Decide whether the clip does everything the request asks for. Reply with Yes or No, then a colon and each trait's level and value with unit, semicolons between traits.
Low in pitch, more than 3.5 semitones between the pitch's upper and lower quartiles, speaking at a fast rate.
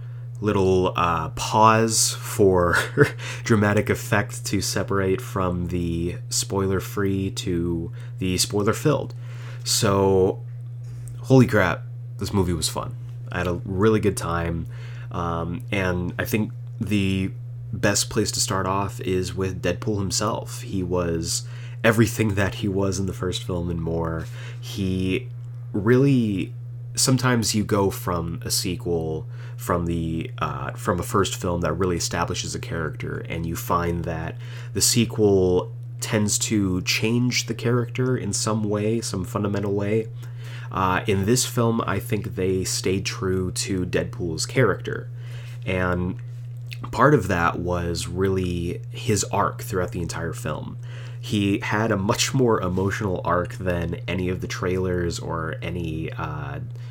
No: low, 110 Hz; average, 4.2 semitones; average, 140 wpm